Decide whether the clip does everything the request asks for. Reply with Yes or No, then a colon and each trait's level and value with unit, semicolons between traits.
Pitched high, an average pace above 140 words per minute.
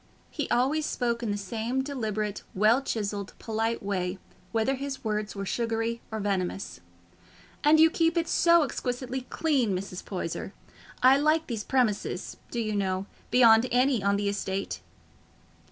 Yes: high, 225 Hz; average, 150 wpm